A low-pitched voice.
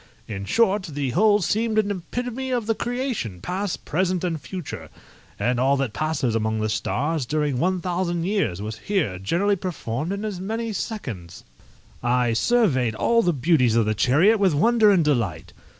No: medium, 170 Hz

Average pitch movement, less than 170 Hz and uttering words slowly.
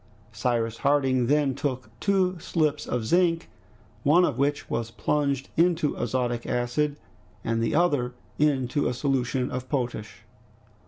Yes: average, 3.6 semitones; low, 135 Hz; slow, 125 wpm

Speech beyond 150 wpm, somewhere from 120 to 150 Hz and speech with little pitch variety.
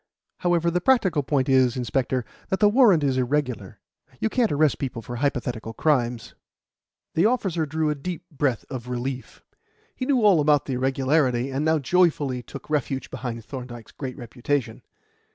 No: average, 160 wpm; medium, 140 Hz; average, 4.3 semitones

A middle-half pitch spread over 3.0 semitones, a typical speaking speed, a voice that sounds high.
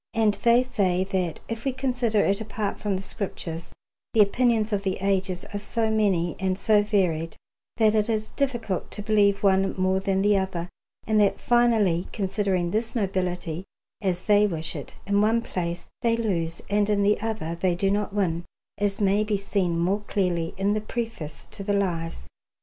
No: average, 2.7 semitones; average, 185 wpm; high, 200 Hz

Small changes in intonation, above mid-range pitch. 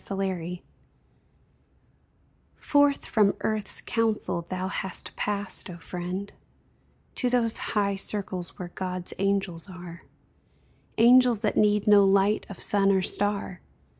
Yes: narrow, 2.3 semitones; high, 200 Hz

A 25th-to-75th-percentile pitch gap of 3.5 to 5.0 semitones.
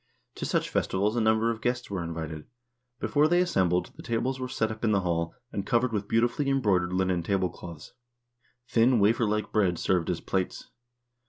Yes: average, 4.6 semitones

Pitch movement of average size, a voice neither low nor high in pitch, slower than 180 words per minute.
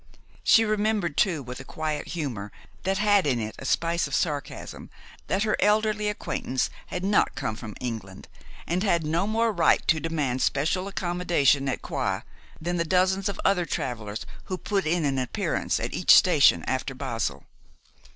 No: wide, 6.3 semitones; medium, 170 Hz; average, 170 wpm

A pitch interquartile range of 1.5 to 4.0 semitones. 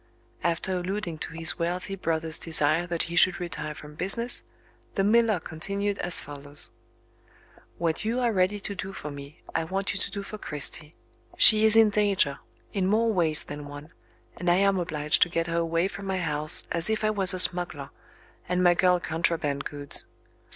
Yes: average, 3.7 semitones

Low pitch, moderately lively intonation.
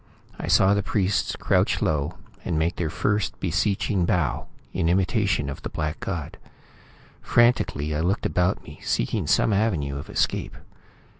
Yes: very low, 90 Hz; average, 4.5 semitones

